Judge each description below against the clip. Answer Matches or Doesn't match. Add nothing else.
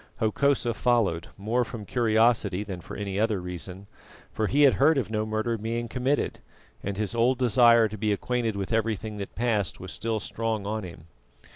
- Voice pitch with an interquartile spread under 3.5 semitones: Matches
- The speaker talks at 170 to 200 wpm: Matches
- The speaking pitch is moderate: Doesn't match